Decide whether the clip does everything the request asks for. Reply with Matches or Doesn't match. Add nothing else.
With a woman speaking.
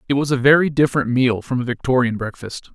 Doesn't match